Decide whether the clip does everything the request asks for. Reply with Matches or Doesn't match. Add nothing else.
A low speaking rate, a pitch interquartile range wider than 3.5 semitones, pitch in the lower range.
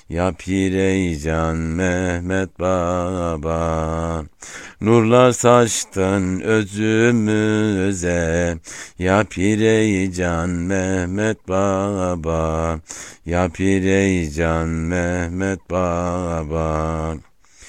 Doesn't match